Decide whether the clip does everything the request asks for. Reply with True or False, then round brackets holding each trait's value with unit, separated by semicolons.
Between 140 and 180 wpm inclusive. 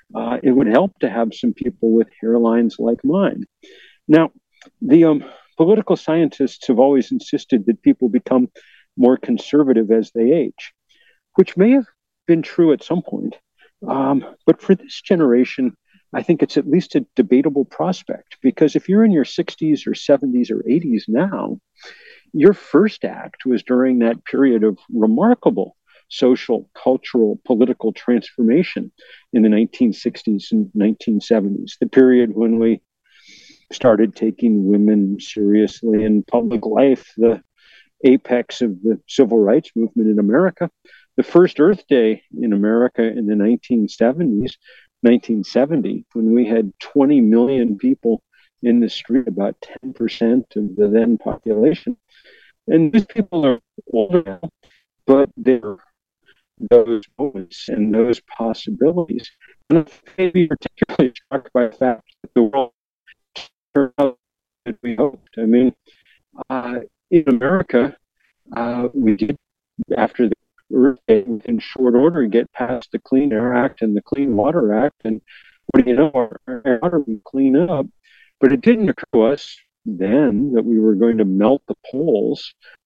True (145 wpm)